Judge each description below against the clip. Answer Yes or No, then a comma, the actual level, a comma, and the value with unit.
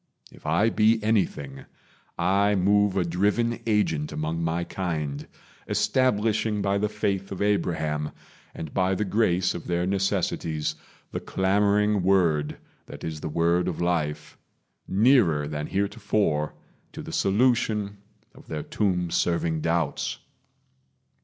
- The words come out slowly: Yes, slow, 125 wpm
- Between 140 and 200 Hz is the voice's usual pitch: No, very low, 95 Hz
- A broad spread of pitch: No, average, 4.2 semitones